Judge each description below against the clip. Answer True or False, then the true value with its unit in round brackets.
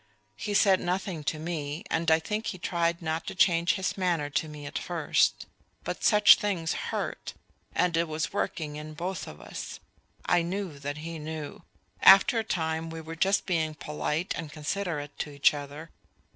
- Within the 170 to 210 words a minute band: True (185 wpm)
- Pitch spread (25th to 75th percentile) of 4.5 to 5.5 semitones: False (2.9 semitones)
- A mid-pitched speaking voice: True (165 Hz)